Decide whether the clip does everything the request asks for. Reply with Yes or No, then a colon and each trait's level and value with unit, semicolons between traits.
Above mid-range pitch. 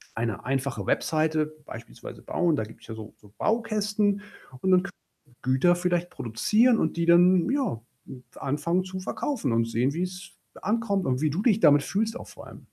No: medium, 175 Hz